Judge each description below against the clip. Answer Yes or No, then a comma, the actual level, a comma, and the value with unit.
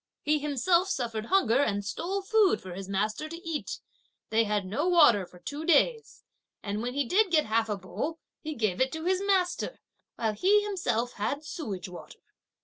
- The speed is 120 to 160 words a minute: No, average, 185 wpm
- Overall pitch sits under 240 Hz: No, very high, 280 Hz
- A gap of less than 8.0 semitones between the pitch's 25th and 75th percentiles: No, wide, 8.6 semitones